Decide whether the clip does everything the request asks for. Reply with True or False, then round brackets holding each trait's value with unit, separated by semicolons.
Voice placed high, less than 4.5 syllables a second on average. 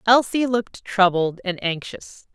True (205 Hz; 4.2 syllables/s)